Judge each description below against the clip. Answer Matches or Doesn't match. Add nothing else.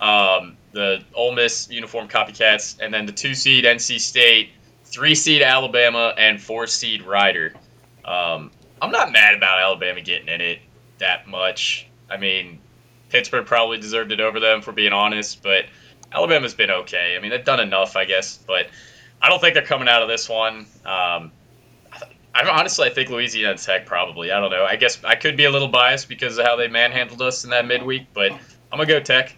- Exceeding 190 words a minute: Matches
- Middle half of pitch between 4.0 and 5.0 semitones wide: Doesn't match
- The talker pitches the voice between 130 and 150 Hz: Doesn't match